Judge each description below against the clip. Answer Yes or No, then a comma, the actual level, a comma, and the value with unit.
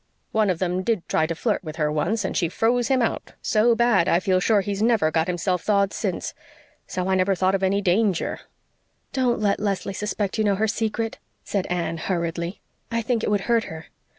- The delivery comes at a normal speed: No, fast, 210 wpm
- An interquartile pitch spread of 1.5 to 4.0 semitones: Yes, average, 3.6 semitones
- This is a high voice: Yes, high, 195 Hz